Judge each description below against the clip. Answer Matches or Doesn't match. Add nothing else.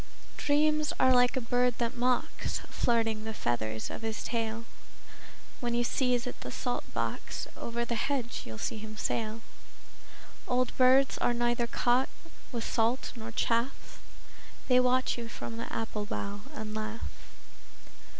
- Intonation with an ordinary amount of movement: Doesn't match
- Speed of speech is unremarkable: Matches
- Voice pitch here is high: Matches